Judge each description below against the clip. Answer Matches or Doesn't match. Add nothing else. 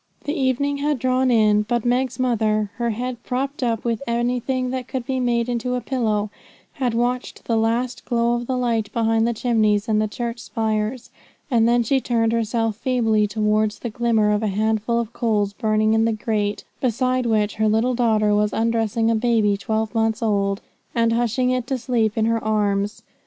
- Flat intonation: Matches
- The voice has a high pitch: Matches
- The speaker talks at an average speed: Matches